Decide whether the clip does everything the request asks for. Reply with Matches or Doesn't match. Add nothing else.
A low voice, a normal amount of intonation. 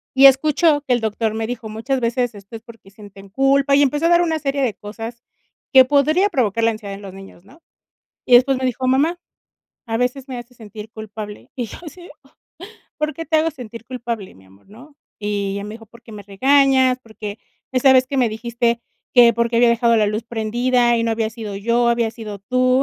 Doesn't match